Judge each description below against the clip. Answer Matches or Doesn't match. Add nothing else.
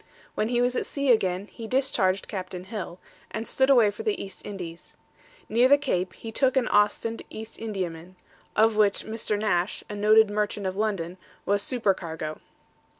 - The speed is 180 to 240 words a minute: Doesn't match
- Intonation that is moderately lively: Matches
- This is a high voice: Matches